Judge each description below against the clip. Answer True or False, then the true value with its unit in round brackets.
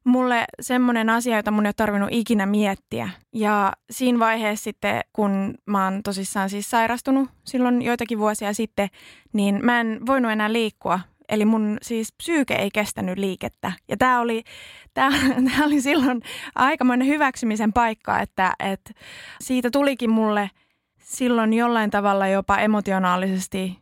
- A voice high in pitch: True (225 Hz)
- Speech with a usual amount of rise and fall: True (3.4 semitones)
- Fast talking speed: False (140 wpm)